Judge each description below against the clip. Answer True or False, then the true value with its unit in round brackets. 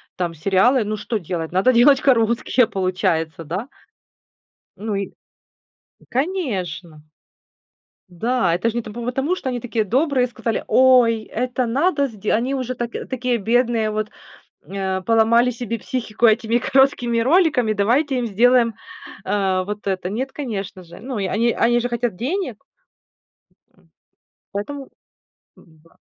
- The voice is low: False (230 Hz)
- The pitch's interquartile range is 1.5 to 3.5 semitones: False (4.2 semitones)